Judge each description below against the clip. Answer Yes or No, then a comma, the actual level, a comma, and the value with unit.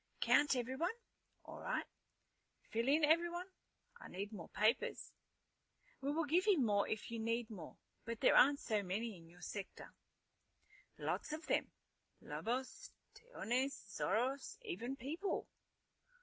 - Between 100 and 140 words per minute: Yes, slow, 135 wpm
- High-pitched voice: Yes, very high, 250 Hz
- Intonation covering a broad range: Yes, wide, 5.9 semitones